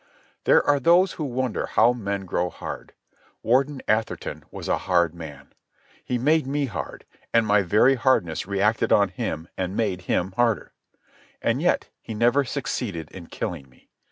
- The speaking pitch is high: No, low, 110 Hz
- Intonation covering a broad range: Yes, wide, 6.2 semitones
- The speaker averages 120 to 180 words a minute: Yes, average, 160 wpm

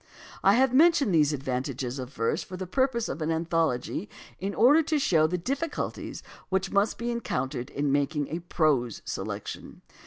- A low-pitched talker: No, medium, 170 Hz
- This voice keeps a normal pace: Yes, average, 165 wpm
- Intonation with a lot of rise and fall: Yes, wide, 8.7 semitones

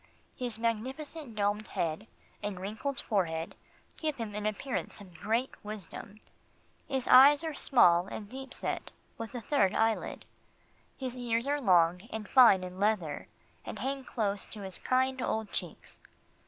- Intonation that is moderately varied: Yes, average, 4.6 semitones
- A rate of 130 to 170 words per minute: Yes, average, 150 wpm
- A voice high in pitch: Yes, high, 220 Hz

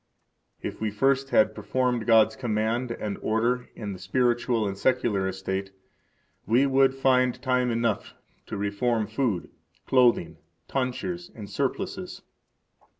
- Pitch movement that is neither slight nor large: Yes, average, 3.4 semitones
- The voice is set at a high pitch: No, low, 115 Hz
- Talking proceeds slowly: Yes, slow, 125 wpm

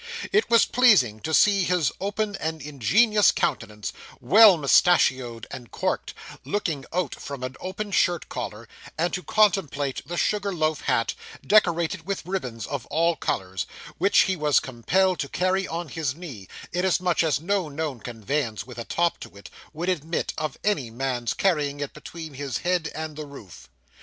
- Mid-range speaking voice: Yes, medium, 160 Hz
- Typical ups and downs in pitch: No, wide, 5.9 semitones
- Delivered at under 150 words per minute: No, average, 165 wpm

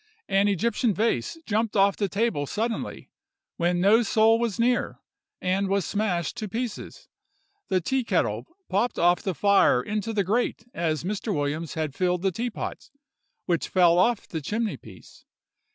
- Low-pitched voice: No, high, 200 Hz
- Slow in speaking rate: No, average, 150 wpm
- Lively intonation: No, average, 4.2 semitones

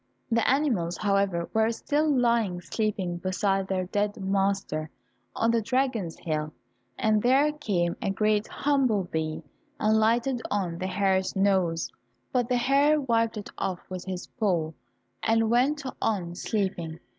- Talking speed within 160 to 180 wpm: No, average, 145 wpm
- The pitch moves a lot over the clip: No, average, 4.3 semitones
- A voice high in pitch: Yes, high, 205 Hz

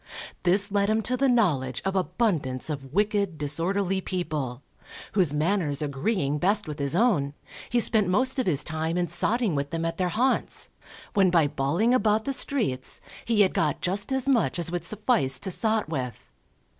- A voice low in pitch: No, medium, 180 Hz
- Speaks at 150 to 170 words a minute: No, average, 180 wpm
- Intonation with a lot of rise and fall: Yes, wide, 6.2 semitones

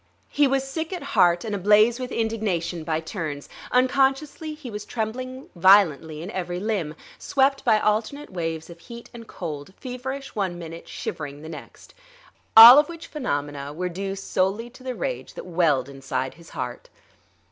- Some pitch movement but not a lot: No, wide, 7.6 semitones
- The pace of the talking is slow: No, average, 165 wpm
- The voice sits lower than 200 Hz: No, high, 205 Hz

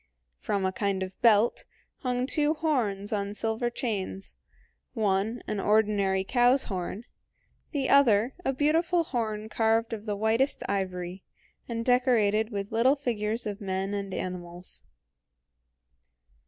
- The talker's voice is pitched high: Yes, high, 215 Hz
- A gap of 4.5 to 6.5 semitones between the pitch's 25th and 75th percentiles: No, average, 3.7 semitones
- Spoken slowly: Yes, slow, 125 wpm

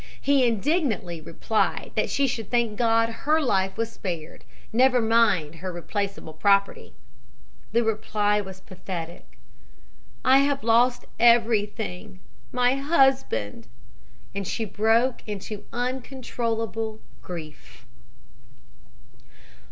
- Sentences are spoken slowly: Yes, slow, 100 wpm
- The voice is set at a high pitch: Yes, high, 225 Hz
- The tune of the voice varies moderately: Yes, average, 4.3 semitones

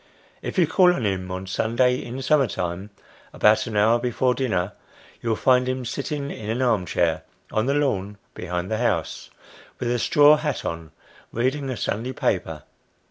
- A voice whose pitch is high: No, low, 120 Hz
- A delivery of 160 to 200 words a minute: Yes, average, 180 wpm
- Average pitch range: Yes, average, 4.7 semitones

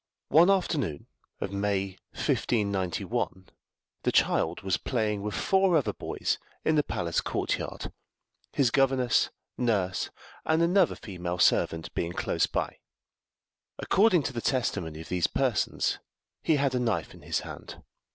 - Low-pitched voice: Yes, low, 115 Hz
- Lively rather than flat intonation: Yes, wide, 8.0 semitones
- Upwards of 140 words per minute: No, slow, 135 wpm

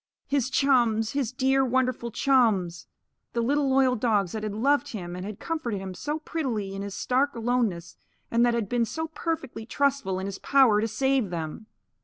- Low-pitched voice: No, high, 235 Hz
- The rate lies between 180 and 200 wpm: Yes, average, 185 wpm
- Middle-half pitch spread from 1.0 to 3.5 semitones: No, average, 4.6 semitones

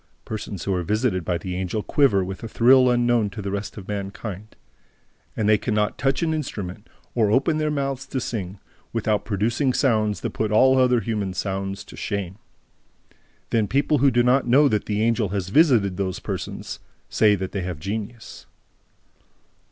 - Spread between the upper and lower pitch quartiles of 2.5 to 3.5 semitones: No, average, 4.1 semitones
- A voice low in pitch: Yes, low, 110 Hz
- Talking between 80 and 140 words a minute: No, average, 180 wpm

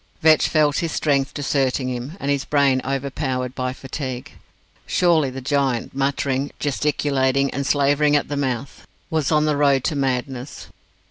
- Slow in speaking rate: No, average, 150 wpm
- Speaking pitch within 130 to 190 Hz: Yes, medium, 140 Hz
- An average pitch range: No, narrow, 1.9 semitones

